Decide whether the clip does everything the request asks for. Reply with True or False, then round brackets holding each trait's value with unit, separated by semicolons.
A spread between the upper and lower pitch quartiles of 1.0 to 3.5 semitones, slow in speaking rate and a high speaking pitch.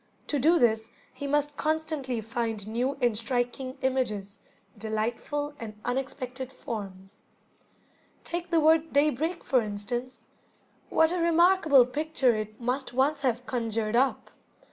False (4.6 semitones; 125 wpm; 255 Hz)